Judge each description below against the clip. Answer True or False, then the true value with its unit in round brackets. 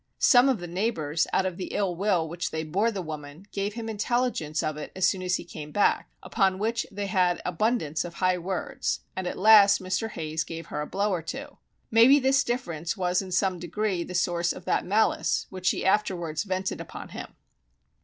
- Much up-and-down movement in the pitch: False (3.7 semitones)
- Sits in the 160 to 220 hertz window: True (185 Hz)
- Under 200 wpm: False (205 wpm)